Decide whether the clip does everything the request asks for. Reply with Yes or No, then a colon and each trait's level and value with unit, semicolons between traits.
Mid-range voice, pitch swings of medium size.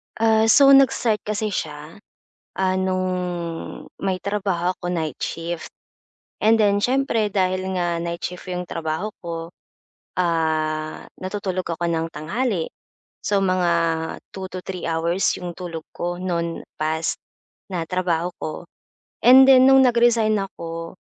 Yes: medium, 180 Hz; average, 3.6 semitones